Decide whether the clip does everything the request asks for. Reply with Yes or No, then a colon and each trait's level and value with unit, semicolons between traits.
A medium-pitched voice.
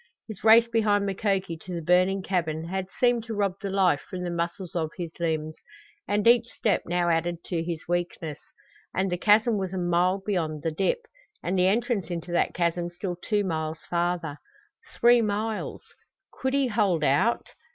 Yes: medium, 180 Hz